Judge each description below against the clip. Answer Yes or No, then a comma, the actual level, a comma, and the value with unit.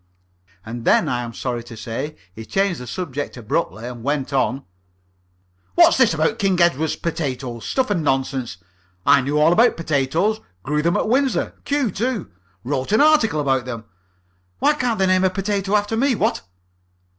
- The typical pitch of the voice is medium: Yes, medium, 155 Hz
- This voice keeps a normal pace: Yes, average, 170 wpm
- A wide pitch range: Yes, wide, 8.0 semitones